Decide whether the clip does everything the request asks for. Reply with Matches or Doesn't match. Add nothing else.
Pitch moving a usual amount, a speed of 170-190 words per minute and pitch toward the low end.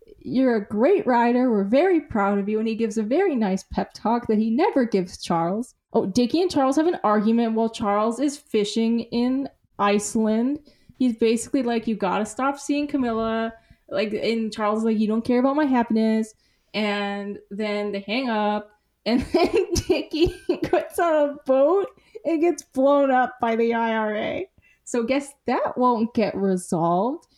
Doesn't match